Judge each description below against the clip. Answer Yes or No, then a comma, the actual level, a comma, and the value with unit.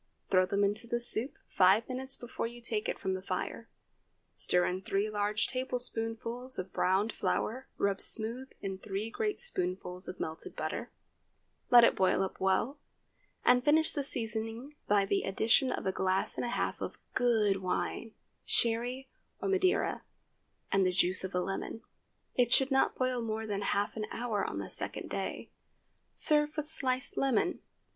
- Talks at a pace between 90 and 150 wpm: No, average, 165 wpm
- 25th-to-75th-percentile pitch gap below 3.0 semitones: No, average, 4.6 semitones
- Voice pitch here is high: Yes, high, 225 Hz